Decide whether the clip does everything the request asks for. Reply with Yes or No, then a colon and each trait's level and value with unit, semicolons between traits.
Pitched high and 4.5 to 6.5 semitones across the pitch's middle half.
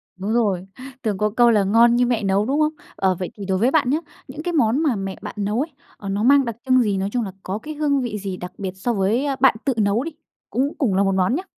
Yes: high, 220 Hz; average, 5.0 semitones